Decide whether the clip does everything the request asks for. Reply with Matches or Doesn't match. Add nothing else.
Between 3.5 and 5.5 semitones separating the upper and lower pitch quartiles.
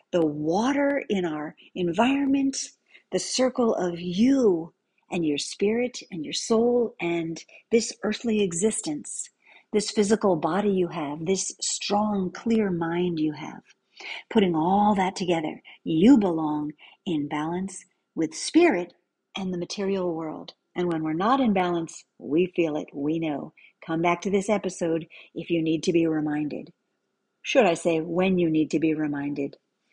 Matches